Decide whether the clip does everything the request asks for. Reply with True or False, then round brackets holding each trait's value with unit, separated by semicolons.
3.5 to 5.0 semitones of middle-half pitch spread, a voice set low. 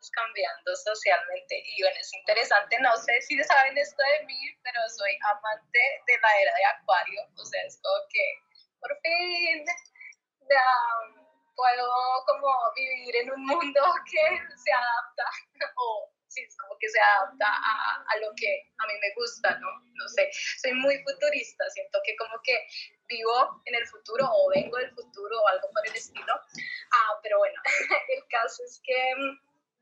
False (4.6 semitones; 275 Hz)